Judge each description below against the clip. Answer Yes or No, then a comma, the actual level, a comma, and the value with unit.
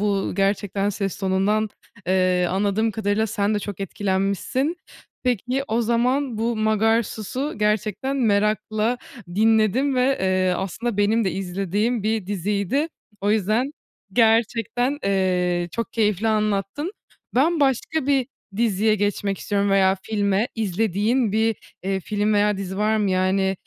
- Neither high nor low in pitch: No, high, 210 Hz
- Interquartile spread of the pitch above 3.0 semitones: No, average, 2.7 semitones